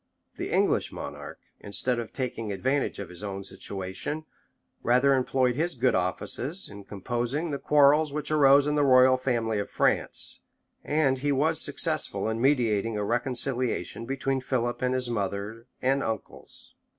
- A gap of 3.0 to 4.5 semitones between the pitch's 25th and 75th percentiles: Yes, average, 3.7 semitones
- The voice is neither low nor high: No, low, 125 Hz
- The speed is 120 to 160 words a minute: Yes, average, 150 wpm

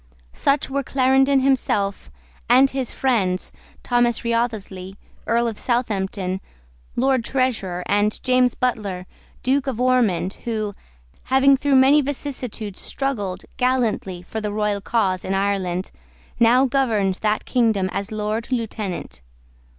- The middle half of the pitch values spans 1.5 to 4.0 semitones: No, average, 4.5 semitones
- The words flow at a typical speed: No, slow, 120 wpm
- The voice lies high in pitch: Yes, high, 230 Hz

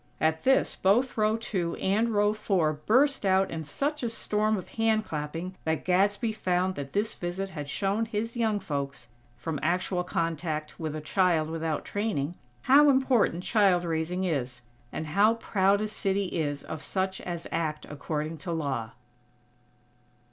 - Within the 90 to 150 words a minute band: No, average, 160 wpm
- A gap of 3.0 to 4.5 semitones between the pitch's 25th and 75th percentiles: No, average, 5.2 semitones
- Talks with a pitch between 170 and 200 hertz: Yes, medium, 185 Hz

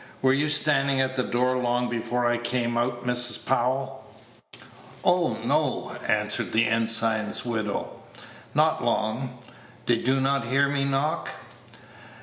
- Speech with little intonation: Yes, narrow, 2.2 semitones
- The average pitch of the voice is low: Yes, low, 125 Hz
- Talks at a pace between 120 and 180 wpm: Yes, slow, 135 wpm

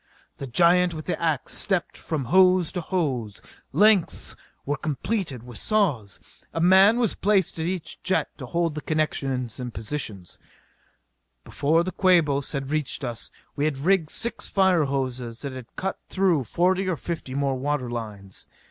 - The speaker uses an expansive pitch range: Yes, wide, 5.9 semitones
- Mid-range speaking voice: Yes, medium, 155 Hz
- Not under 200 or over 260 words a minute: No, average, 165 wpm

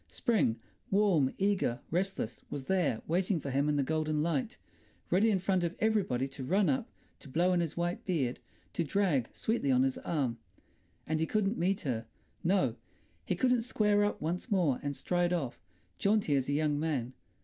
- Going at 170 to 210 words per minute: Yes, average, 175 wpm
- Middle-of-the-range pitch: Yes, medium, 170 Hz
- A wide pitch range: Yes, wide, 5.9 semitones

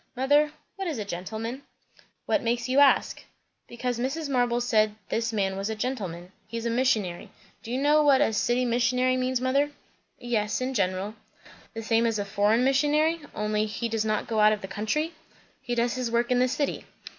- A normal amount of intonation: Yes, average, 3.3 semitones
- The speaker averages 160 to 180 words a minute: No, average, 190 wpm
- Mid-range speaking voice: No, high, 235 Hz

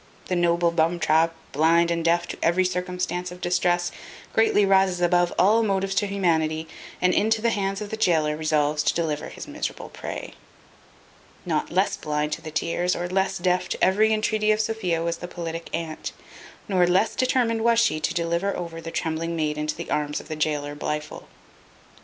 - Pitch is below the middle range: No, medium, 175 Hz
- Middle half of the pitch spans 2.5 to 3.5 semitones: Yes, average, 3.2 semitones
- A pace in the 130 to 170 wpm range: No, average, 185 wpm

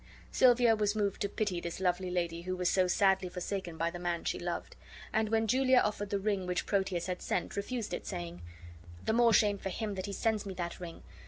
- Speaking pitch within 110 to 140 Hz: No, high, 195 Hz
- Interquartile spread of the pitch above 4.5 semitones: No, average, 3.0 semitones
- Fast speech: Yes, fast, 225 wpm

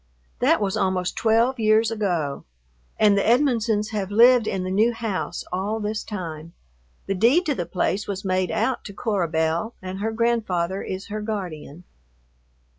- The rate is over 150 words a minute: Yes, average, 165 wpm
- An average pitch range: Yes, average, 3.3 semitones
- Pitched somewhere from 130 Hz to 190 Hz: No, high, 205 Hz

